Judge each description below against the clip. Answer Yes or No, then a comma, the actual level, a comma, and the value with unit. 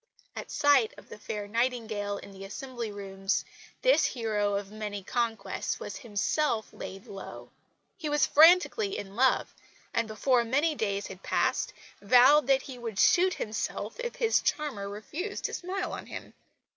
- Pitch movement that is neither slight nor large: No, wide, 6.3 semitones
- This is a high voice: Yes, high, 230 Hz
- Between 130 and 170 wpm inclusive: Yes, average, 160 wpm